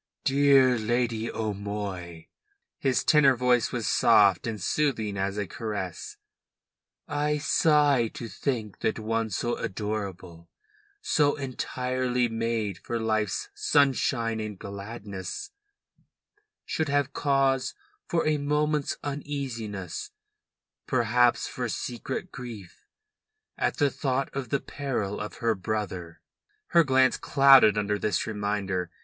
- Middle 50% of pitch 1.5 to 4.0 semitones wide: No, average, 4.8 semitones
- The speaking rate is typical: No, slow, 115 wpm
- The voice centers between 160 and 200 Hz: No, low, 115 Hz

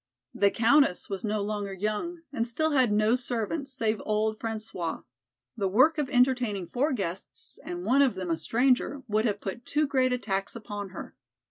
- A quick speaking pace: No, average, 185 wpm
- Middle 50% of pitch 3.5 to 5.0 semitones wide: Yes, average, 4.1 semitones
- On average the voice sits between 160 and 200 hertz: No, high, 220 Hz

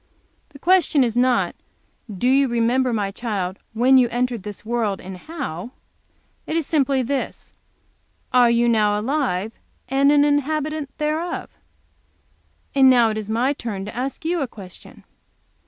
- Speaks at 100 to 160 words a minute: Yes, average, 150 wpm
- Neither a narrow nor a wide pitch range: Yes, average, 4.3 semitones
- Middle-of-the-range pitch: No, very high, 250 Hz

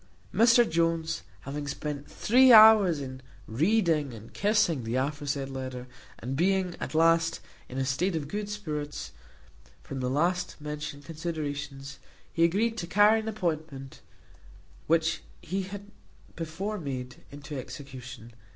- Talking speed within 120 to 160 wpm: Yes, slow, 135 wpm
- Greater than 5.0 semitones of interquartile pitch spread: Yes, wide, 5.4 semitones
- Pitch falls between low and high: Yes, medium, 155 Hz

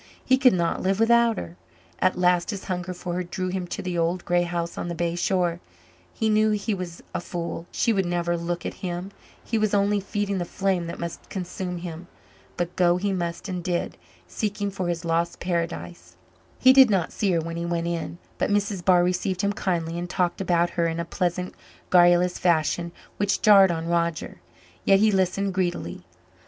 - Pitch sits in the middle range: Yes, medium, 180 Hz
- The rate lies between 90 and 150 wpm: No, average, 200 wpm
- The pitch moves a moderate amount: No, narrow, 2.2 semitones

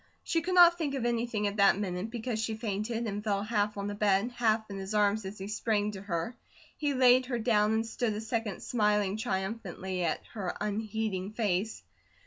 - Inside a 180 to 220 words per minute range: Yes, average, 200 wpm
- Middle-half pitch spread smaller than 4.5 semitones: Yes, narrow, 2.4 semitones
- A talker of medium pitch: No, high, 215 Hz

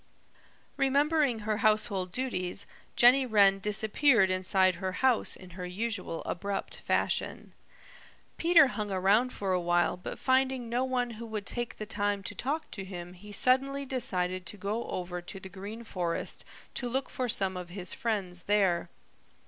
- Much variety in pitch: No, average, 4.9 semitones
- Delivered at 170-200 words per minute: No, average, 160 wpm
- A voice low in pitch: No, high, 205 Hz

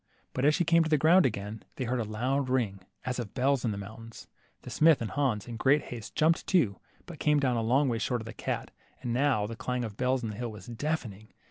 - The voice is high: No, low, 125 Hz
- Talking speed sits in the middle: No, fast, 255 wpm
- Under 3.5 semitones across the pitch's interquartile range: No, average, 4.2 semitones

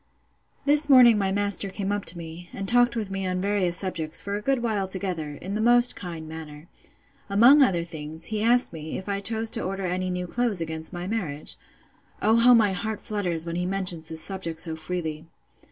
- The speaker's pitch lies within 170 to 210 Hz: Yes, high, 190 Hz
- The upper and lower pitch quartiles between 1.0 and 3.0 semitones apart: No, average, 4.4 semitones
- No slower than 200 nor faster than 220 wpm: Yes, fast, 205 wpm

